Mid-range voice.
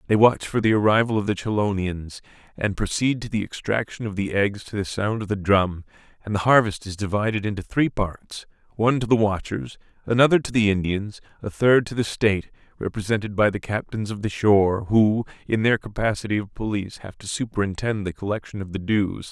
No: low, 105 Hz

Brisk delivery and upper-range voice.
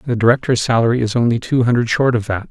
No: fast, 240 wpm; low, 120 Hz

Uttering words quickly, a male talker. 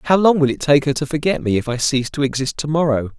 Yes: fast, 300 wpm; male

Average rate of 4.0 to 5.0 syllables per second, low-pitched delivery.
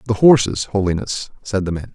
No: 5.4 syllables/s; low, 105 Hz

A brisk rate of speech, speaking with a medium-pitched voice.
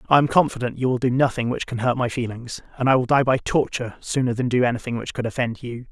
No: fast, 275 wpm; low, 125 Hz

